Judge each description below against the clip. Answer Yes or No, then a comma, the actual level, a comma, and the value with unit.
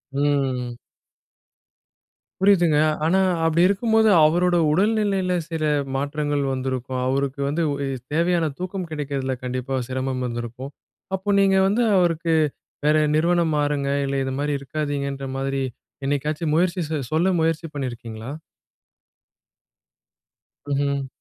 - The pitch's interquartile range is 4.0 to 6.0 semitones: Yes, average, 4.3 semitones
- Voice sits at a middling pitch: Yes, medium, 150 Hz